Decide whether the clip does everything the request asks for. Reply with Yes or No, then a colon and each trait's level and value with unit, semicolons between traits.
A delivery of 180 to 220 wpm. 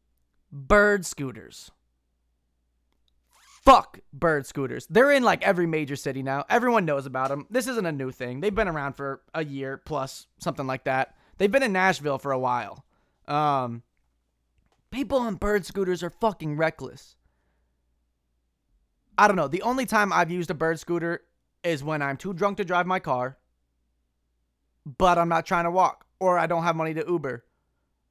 No: average, 170 wpm